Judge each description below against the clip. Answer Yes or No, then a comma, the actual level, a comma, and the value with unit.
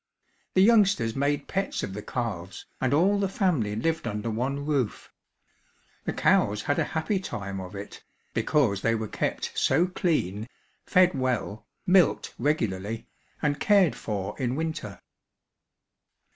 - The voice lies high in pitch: No, low, 130 Hz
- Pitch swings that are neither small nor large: No, wide, 7.6 semitones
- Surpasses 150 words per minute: No, average, 140 wpm